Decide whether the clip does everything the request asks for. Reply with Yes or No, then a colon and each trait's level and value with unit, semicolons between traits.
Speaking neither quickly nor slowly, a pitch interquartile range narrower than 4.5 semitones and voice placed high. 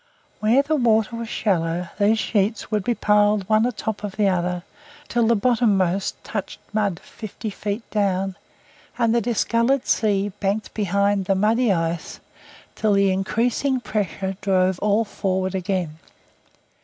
Yes: average, 145 wpm; average, 2.8 semitones; high, 205 Hz